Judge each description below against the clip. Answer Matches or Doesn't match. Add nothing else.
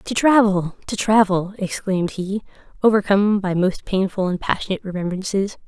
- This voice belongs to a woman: Matches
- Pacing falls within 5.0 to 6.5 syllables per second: Matches